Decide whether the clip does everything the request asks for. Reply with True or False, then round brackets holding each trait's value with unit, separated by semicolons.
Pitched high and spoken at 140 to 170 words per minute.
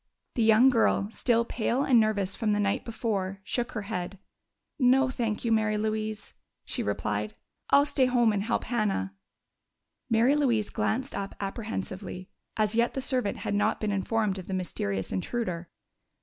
True (215 Hz; 165 wpm)